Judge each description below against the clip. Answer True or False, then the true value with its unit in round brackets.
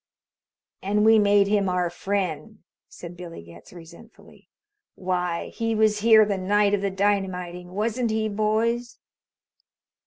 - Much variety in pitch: False (3.1 semitones)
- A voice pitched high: True (200 Hz)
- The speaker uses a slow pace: True (130 wpm)